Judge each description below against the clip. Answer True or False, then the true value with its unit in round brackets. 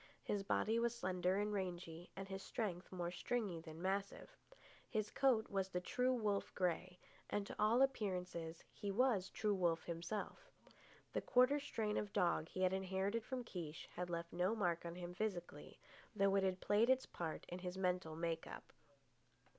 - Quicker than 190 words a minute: False (175 wpm)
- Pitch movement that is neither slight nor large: True (3.4 semitones)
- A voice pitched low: False (190 Hz)